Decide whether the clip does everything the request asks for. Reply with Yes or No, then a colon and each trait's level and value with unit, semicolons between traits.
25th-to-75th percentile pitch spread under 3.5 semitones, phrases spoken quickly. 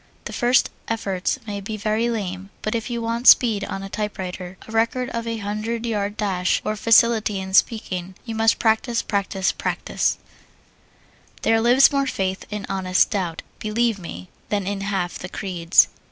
No: average, 3.0 semitones; average, 170 wpm